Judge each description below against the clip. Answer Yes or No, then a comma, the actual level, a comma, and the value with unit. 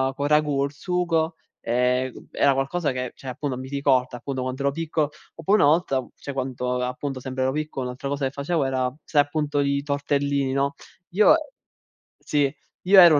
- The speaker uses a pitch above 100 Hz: Yes, medium, 140 Hz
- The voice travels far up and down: No, narrow, 2.4 semitones